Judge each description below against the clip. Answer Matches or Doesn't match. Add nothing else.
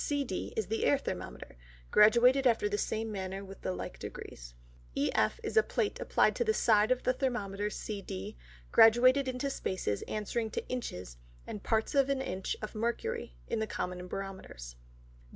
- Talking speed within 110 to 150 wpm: Doesn't match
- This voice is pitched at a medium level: Doesn't match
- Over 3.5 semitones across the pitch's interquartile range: Matches